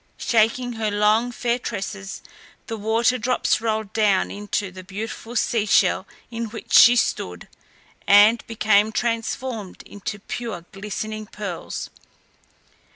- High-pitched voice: Yes, high, 215 Hz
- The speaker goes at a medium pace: No, slow, 120 wpm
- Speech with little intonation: Yes, narrow, 2.1 semitones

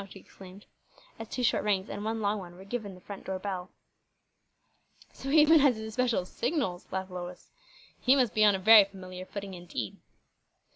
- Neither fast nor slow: Yes, average, 190 wpm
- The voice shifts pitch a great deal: No, average, 3.3 semitones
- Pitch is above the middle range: Yes, high, 200 Hz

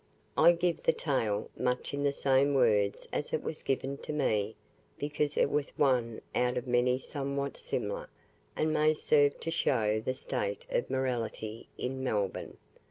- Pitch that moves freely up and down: No, average, 3.7 semitones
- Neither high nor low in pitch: No, low, 130 Hz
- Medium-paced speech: Yes, average, 165 wpm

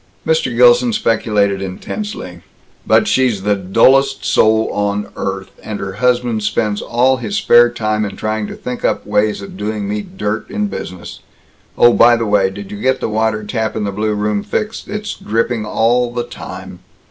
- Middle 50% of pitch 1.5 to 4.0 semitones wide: Yes, average, 2.9 semitones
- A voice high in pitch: No, low, 110 Hz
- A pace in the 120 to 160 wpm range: No, average, 180 wpm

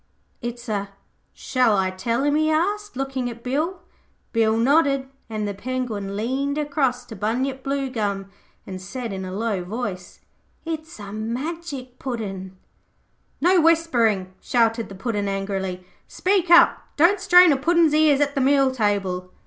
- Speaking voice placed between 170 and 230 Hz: No, high, 245 Hz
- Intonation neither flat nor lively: No, wide, 6.1 semitones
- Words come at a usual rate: Yes, average, 150 wpm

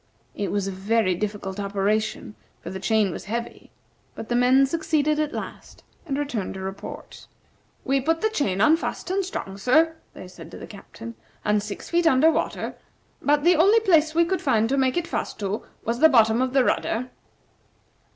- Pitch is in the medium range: No, very high, 250 Hz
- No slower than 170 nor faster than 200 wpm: Yes, average, 190 wpm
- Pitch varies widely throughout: Yes, wide, 7.1 semitones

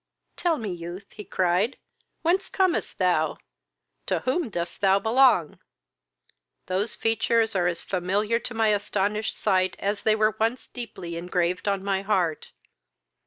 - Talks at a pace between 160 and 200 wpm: No, average, 140 wpm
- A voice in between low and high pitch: No, high, 200 Hz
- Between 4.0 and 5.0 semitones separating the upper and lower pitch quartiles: No, average, 3.6 semitones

